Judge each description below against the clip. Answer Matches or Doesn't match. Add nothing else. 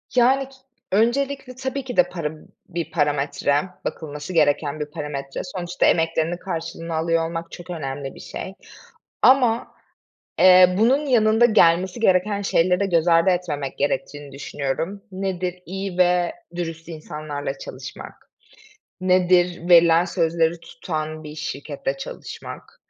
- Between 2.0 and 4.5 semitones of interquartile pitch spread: Matches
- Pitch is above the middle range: Doesn't match